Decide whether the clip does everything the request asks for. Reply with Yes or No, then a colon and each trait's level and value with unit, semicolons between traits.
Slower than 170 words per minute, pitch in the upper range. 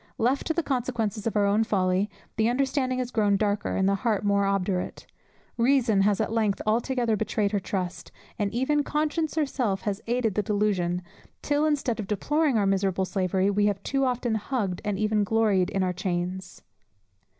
No: average, 180 wpm; high, 210 Hz